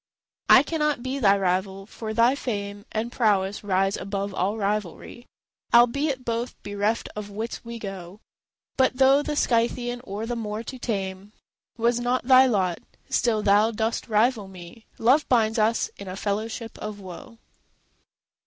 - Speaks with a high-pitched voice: Yes, high, 220 Hz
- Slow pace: No, average, 155 wpm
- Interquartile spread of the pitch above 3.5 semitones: No, average, 3.2 semitones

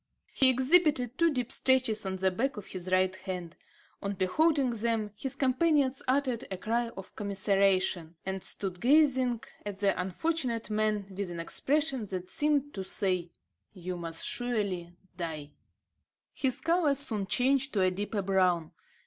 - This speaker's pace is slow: No, average, 150 wpm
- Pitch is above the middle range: Yes, high, 210 Hz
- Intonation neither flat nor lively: No, wide, 5.8 semitones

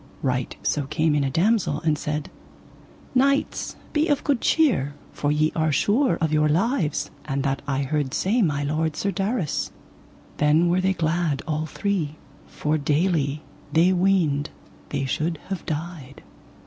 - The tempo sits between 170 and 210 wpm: No, average, 155 wpm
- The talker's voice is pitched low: No, medium, 155 Hz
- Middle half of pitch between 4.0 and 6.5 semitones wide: Yes, average, 4.3 semitones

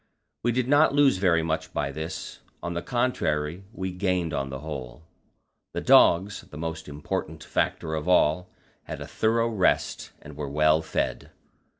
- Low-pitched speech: Yes, very low, 80 Hz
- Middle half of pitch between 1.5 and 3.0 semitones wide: No, average, 4.3 semitones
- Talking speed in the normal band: Yes, average, 165 wpm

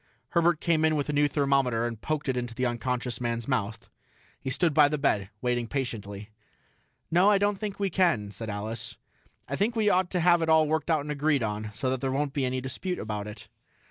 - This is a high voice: No, low, 135 Hz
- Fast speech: Yes, fast, 220 wpm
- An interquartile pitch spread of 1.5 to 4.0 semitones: No, wide, 5.4 semitones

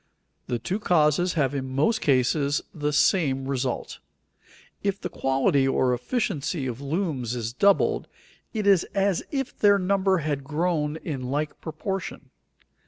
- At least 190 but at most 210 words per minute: No, average, 140 wpm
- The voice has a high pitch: No, medium, 150 Hz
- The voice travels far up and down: Yes, wide, 5.9 semitones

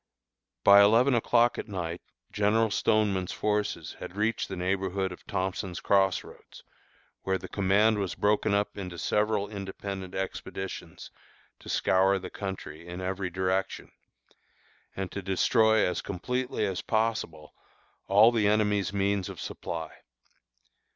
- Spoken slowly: Yes, slow, 130 wpm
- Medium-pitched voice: No, low, 100 Hz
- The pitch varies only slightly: Yes, narrow, 2.1 semitones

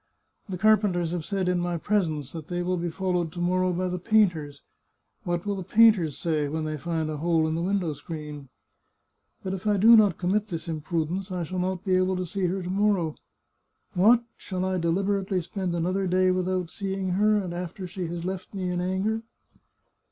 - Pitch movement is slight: Yes, narrow, 2.3 semitones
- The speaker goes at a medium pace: No, fast, 210 wpm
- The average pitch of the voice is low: No, medium, 180 Hz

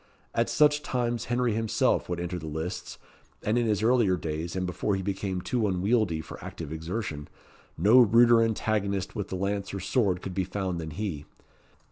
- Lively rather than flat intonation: No, average, 4.2 semitones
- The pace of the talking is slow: No, average, 180 wpm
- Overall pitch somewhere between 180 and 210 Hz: No, low, 100 Hz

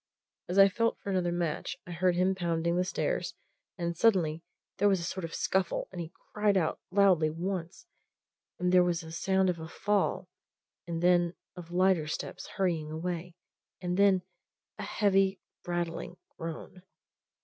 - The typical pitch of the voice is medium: Yes, medium, 180 Hz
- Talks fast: No, average, 160 wpm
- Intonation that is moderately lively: No, narrow, 2.1 semitones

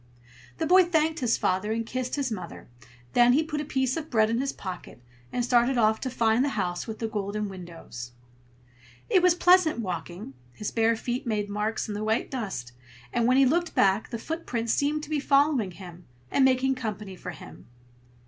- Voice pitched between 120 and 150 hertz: No, high, 230 Hz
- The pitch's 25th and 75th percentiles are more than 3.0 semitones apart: Yes, average, 5.0 semitones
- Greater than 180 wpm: Yes, average, 195 wpm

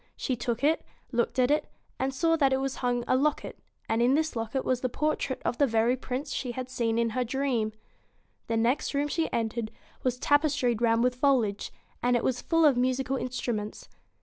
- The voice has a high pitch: Yes, very high, 250 Hz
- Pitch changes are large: No, narrow, 2.6 semitones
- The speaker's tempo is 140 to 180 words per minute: No, average, 200 wpm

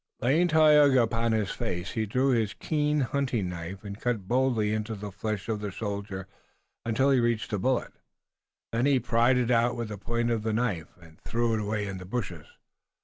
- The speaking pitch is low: Yes, low, 115 Hz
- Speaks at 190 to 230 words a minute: Yes, average, 200 wpm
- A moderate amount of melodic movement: Yes, average, 3.4 semitones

